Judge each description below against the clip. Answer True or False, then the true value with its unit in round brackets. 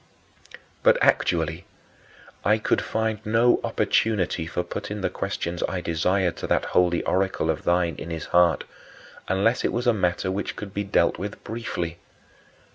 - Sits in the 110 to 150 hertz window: False (95 Hz)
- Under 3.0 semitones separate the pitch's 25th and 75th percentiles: False (3.5 semitones)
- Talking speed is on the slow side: False (160 wpm)